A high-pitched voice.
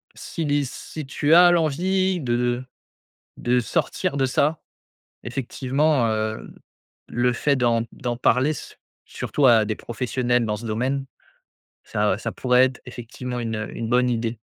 No: low, 125 Hz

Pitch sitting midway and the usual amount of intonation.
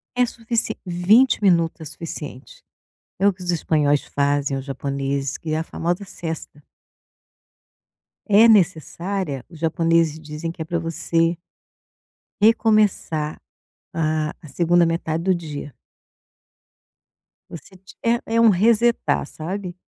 Yes: medium, 170 Hz; average, 4.3 semitones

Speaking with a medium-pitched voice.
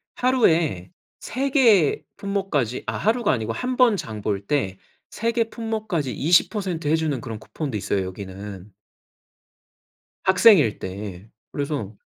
Yes: medium, 150 Hz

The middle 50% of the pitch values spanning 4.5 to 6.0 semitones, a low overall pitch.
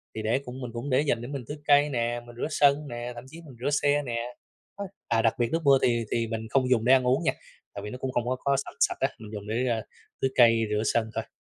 No: average, 2.9 semitones; low, 125 Hz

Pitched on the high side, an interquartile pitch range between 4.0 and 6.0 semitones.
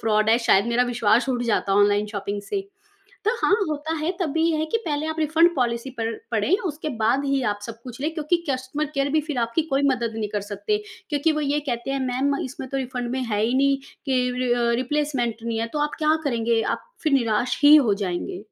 Yes: very high, 260 Hz; average, 4.5 semitones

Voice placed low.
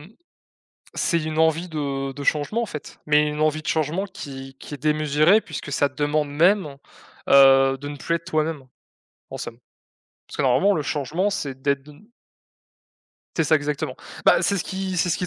No: medium, 150 Hz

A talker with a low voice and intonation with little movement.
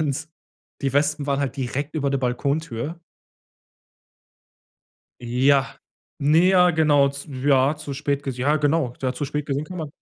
No: medium, 145 Hz; narrow, 2.1 semitones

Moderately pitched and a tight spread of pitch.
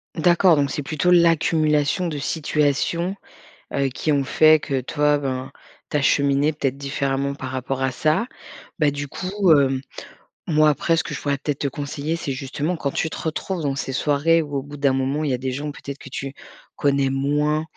Yes: medium, 145 Hz; narrow, 2.2 semitones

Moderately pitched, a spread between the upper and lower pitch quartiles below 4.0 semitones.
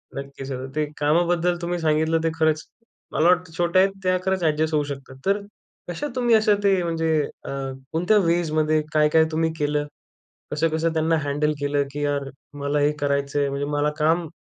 Yes: medium, 155 Hz; average, 2.7 semitones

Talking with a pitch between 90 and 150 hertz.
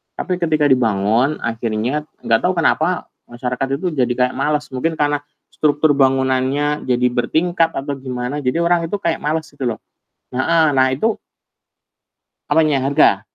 Yes: medium, 140 Hz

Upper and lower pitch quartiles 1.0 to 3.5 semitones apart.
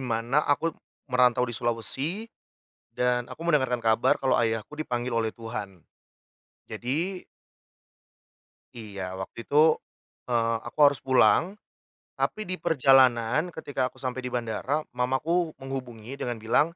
No: average, 4.0 semitones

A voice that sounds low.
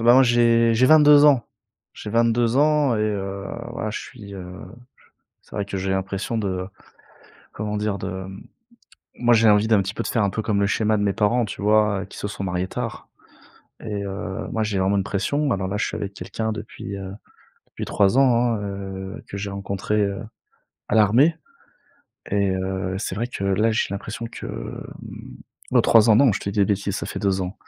Yes: low, 105 Hz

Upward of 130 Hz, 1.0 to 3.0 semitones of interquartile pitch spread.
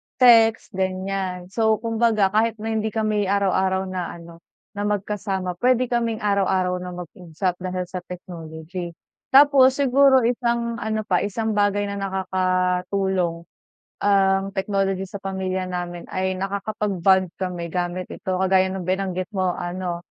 Yes: high, 190 Hz; average, 2.7 semitones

